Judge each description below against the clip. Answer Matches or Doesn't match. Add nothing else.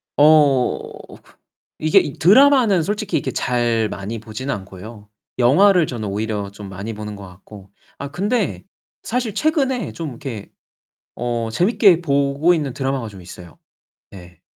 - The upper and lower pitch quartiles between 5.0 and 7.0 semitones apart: Doesn't match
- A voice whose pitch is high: Doesn't match